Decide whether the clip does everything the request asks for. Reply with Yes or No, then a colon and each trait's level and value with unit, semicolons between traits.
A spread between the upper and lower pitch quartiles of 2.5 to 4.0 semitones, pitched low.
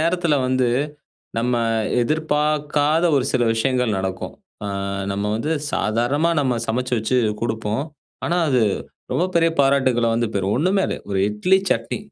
No: average, 4.9 semitones; low, 130 Hz